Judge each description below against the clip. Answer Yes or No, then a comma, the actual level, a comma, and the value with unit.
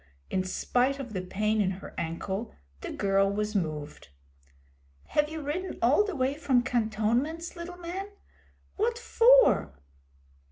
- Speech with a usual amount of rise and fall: No, wide, 9.0 semitones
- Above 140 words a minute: No, slow, 135 wpm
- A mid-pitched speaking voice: No, high, 245 Hz